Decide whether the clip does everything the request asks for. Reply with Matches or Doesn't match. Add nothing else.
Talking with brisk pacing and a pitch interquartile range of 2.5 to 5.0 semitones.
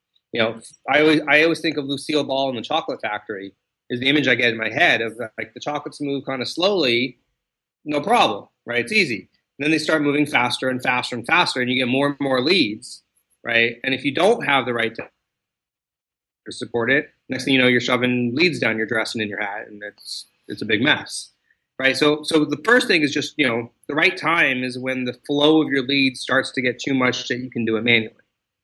Matches